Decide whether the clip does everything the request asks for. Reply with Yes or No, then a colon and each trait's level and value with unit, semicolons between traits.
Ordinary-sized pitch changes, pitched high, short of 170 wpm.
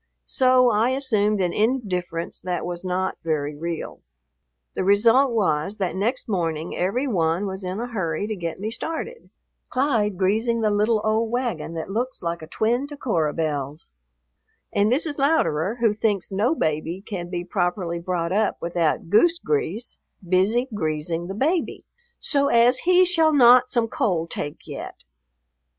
No: wide, 5.9 semitones; high, 205 Hz; average, 160 wpm